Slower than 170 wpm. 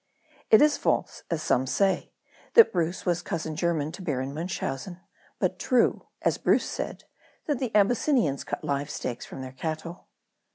Yes: average, 160 wpm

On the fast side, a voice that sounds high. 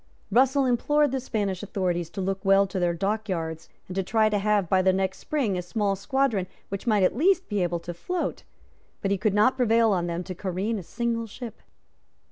Yes: fast, 210 wpm; high, 200 Hz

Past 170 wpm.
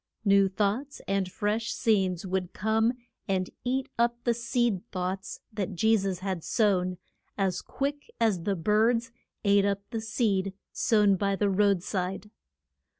No: average, 150 wpm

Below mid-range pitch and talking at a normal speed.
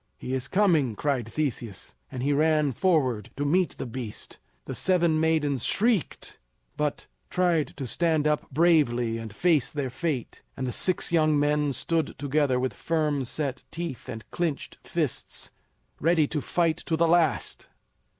No: medium, 150 Hz; average, 155 wpm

